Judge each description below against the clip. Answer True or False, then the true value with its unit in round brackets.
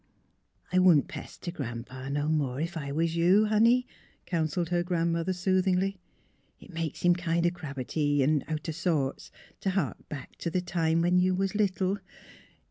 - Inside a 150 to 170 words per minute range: False (180 wpm)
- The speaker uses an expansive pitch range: False (3.3 semitones)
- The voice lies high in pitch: False (170 Hz)